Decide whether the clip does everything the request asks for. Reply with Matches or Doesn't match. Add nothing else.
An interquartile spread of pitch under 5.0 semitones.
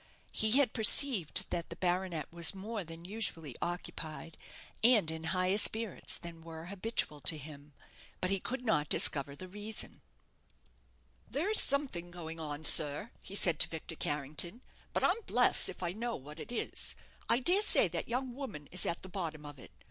Doesn't match